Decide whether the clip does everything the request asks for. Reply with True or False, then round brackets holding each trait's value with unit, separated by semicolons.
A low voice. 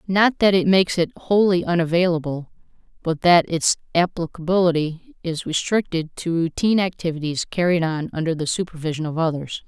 False (170 Hz)